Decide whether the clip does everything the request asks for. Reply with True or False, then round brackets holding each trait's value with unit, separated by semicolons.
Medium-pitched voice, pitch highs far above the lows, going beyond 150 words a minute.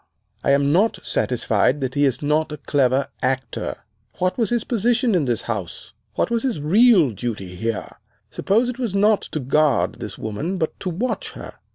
True (150 Hz; 8.7 semitones; 185 wpm)